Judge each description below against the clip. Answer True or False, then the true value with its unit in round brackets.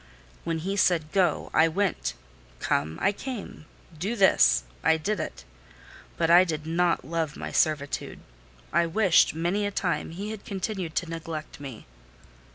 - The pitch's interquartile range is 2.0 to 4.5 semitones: True (3.6 semitones)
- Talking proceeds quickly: False (155 wpm)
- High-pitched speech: False (170 Hz)